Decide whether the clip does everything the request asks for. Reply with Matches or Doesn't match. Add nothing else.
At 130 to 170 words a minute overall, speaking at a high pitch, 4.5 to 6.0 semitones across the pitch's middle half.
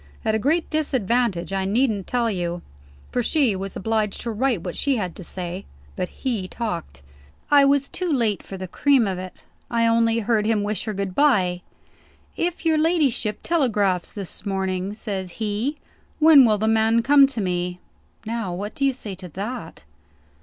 Doesn't match